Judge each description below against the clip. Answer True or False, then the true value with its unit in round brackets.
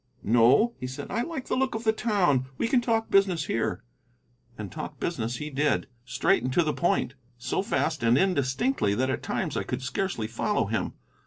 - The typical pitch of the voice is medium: True (150 Hz)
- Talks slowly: False (195 wpm)